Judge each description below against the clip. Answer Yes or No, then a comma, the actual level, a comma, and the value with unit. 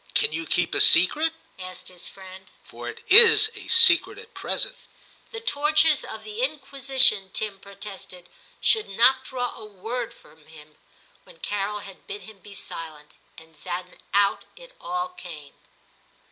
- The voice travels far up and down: Yes, wide, 8.8 semitones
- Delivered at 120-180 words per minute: Yes, average, 175 wpm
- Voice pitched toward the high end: Yes, high, 215 Hz